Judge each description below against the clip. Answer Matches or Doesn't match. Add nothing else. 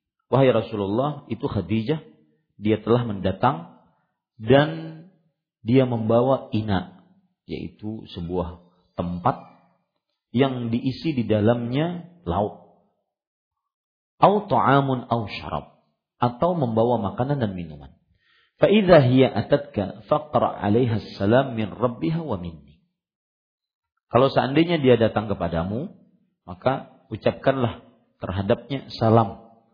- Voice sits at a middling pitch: Doesn't match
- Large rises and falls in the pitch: Matches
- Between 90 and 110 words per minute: Doesn't match